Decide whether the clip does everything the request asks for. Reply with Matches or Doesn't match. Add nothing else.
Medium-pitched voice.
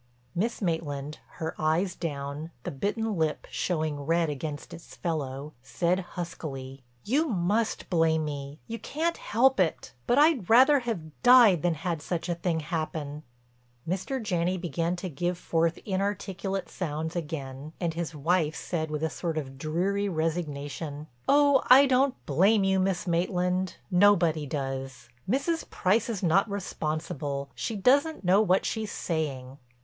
Matches